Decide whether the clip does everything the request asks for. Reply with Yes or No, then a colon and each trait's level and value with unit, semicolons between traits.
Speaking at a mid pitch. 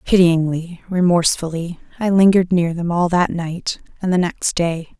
Yes: medium, 175 Hz